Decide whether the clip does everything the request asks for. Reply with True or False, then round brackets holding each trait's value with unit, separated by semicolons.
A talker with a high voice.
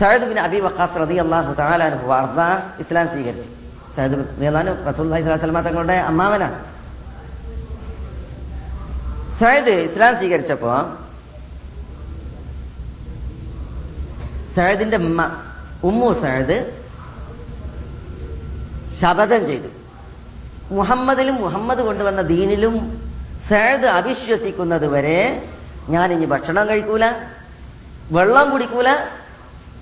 False (165 Hz)